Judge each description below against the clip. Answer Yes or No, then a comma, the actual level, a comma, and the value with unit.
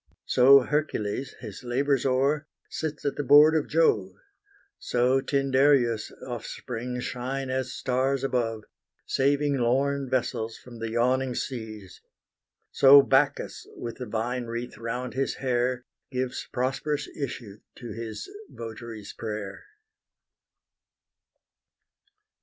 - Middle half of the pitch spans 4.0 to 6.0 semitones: No, average, 2.7 semitones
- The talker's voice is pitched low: Yes, low, 125 Hz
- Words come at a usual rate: No, slow, 110 wpm